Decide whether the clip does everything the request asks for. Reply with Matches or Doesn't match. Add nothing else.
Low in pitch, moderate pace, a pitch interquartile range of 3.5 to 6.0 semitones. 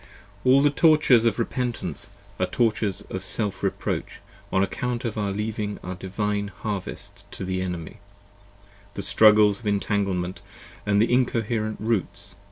Doesn't match